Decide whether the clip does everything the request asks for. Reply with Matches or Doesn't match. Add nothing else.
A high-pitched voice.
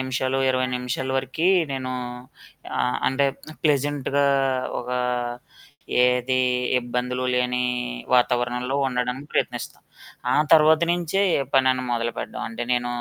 Doesn't match